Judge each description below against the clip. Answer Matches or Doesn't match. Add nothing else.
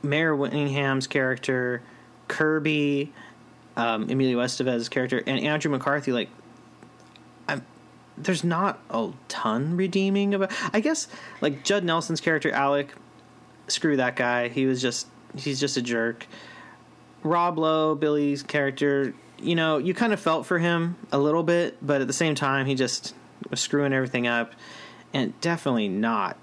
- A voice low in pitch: Doesn't match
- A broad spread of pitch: Doesn't match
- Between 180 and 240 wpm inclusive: Doesn't match